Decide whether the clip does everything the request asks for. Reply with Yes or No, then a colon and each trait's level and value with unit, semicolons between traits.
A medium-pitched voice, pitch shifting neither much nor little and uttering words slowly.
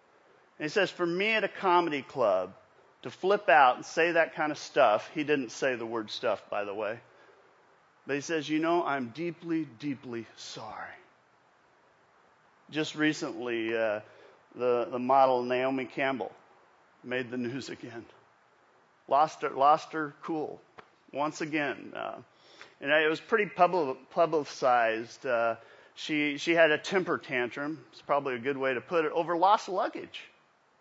No: medium, 150 Hz; average, 4.6 semitones; average, 155 wpm